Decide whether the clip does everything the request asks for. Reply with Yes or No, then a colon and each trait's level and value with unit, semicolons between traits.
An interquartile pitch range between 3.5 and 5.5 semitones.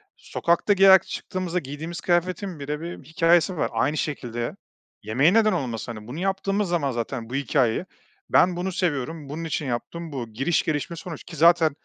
Yes: average, 4.5 semitones